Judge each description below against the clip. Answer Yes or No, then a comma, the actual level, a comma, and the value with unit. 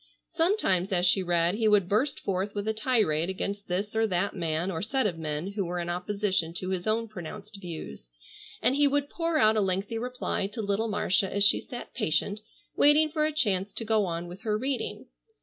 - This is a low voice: No, high, 200 Hz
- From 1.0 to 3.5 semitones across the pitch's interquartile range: No, average, 4.0 semitones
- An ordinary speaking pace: No, fast, 210 wpm